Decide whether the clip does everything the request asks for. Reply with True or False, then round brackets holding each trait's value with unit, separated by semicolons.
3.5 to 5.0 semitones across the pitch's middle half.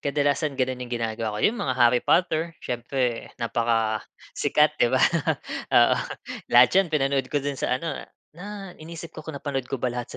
True (4.5 semitones)